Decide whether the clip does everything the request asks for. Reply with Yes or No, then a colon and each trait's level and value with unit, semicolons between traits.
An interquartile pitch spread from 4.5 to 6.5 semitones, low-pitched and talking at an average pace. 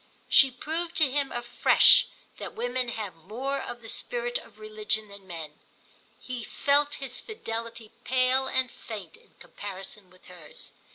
No: average, 4.9 semitones; high, 245 Hz; average, 150 wpm